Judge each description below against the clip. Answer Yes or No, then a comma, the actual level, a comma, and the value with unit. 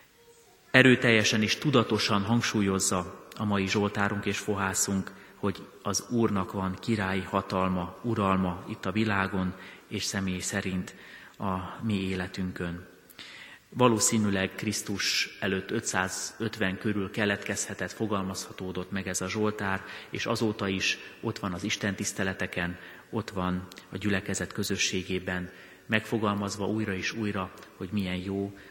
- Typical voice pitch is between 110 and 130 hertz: No, low, 100 Hz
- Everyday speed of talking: Yes, average, 115 wpm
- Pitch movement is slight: Yes, narrow, 2.2 semitones